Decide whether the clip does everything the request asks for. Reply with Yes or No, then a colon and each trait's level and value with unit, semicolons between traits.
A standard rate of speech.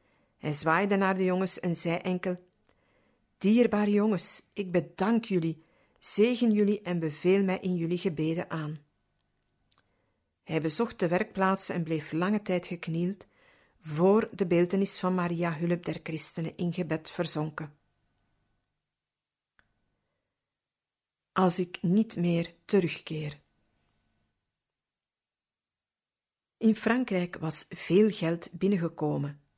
No: slow, 110 wpm